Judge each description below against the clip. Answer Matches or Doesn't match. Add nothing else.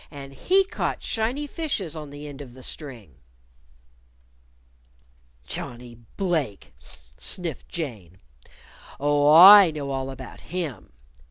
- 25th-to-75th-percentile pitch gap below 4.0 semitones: Doesn't match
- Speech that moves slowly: Matches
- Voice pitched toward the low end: Doesn't match